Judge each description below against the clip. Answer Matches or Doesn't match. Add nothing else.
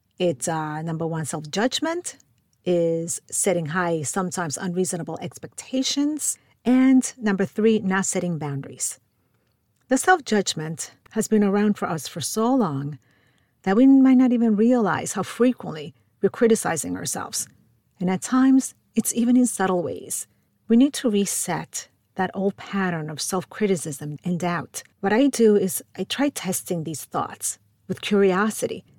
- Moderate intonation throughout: Doesn't match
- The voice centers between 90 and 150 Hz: Doesn't match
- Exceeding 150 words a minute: Doesn't match